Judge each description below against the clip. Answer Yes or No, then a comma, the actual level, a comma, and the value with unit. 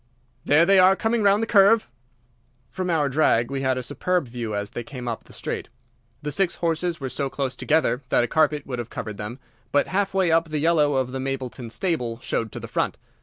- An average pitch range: No, wide, 5.9 semitones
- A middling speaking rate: No, fast, 220 wpm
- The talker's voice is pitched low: No, medium, 145 Hz